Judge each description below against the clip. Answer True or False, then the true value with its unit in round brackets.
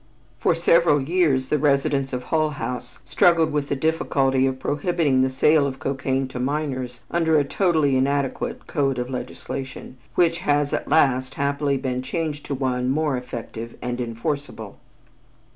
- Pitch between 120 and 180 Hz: True (140 Hz)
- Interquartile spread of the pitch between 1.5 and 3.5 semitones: True (2.6 semitones)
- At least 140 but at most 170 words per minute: True (155 wpm)